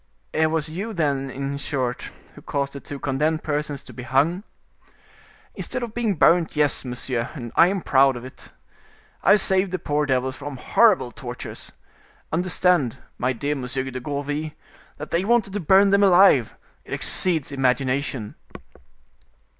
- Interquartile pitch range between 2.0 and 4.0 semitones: No, average, 5.1 semitones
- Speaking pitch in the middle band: Yes, medium, 145 Hz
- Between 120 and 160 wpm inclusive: Yes, average, 155 wpm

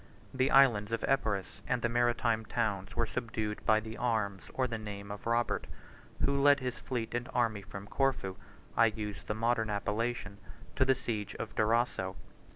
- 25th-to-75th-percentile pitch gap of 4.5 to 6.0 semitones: No, average, 2.7 semitones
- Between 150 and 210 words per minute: Yes, average, 170 wpm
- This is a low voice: Yes, low, 115 Hz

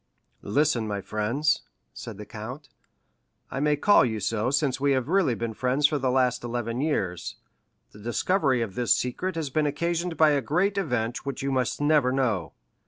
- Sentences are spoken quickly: No, average, 170 wpm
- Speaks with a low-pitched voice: Yes, low, 130 Hz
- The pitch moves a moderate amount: Yes, average, 4.4 semitones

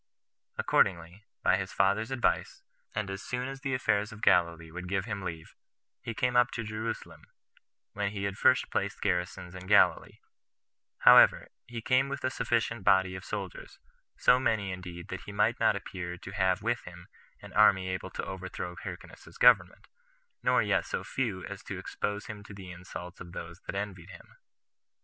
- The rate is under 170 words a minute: No, average, 175 wpm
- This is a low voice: Yes, low, 100 Hz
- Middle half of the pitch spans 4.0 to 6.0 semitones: No, average, 3.4 semitones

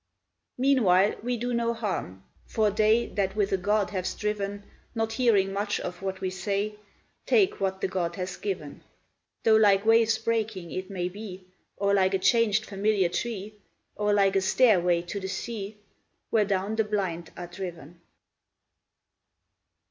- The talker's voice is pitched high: Yes, high, 200 Hz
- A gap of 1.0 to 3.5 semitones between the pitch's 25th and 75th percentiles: Yes, narrow, 2.6 semitones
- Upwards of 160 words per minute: No, average, 155 wpm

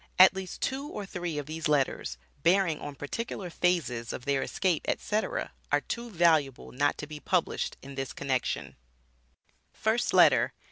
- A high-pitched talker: No, medium, 165 Hz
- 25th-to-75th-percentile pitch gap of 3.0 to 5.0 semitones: No, wide, 5.4 semitones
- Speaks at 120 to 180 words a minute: Yes, average, 155 wpm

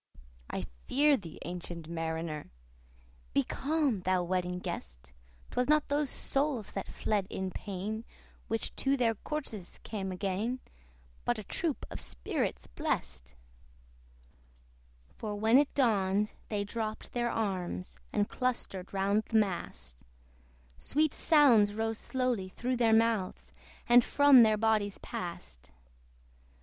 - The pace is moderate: No, slow, 125 wpm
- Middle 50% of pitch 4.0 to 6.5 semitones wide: Yes, average, 5.1 semitones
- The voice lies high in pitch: Yes, high, 210 Hz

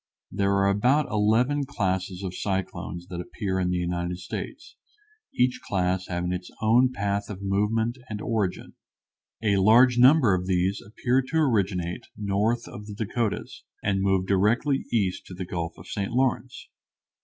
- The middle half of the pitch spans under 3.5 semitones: No, average, 4.1 semitones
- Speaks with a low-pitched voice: Yes, low, 100 Hz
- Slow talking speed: No, average, 155 wpm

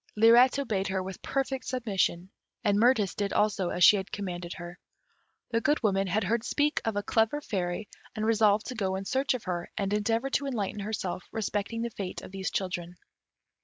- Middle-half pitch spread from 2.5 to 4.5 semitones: Yes, average, 3.3 semitones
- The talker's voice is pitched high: Yes, high, 205 Hz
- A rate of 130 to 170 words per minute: No, average, 195 wpm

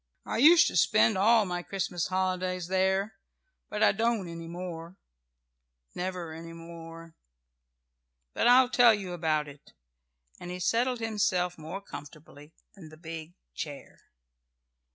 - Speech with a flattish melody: No, average, 3.7 semitones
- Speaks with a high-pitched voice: No, medium, 180 Hz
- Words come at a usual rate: No, slow, 130 wpm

